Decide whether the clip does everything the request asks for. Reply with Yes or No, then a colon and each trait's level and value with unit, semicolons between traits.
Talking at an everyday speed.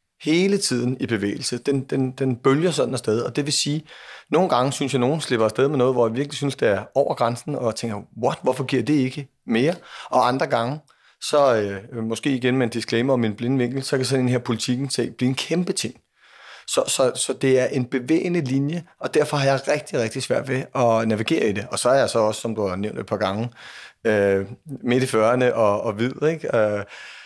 No: fast, 230 wpm